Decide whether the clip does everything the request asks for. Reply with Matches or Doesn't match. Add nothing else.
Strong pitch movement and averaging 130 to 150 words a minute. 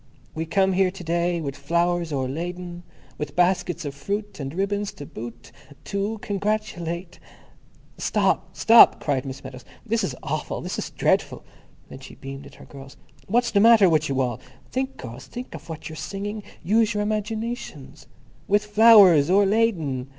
Doesn't match